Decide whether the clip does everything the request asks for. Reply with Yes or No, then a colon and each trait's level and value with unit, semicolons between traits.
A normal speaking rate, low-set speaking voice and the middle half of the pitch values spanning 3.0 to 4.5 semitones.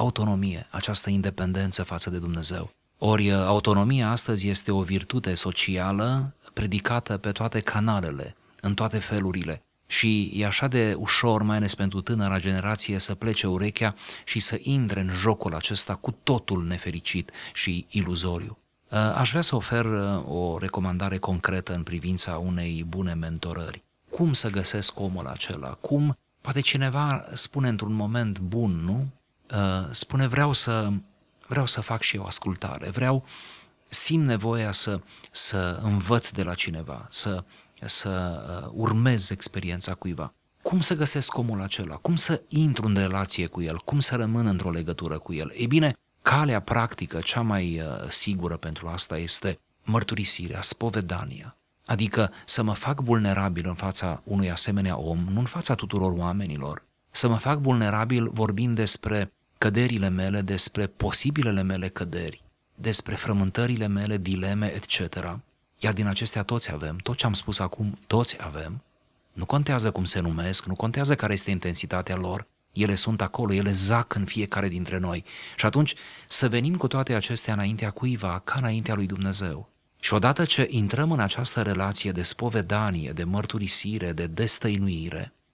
Yes: average, 150 wpm; low, 100 Hz; average, 3.9 semitones